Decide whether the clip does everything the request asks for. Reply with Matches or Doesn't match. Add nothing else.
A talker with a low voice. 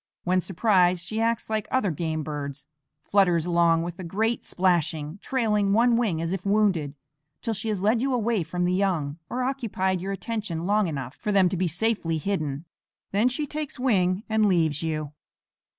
Doesn't match